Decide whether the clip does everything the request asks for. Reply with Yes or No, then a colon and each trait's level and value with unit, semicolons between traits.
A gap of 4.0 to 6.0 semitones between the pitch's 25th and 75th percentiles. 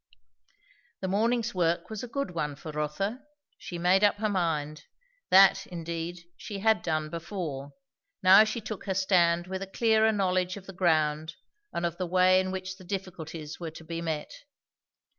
No: average, 3.1 semitones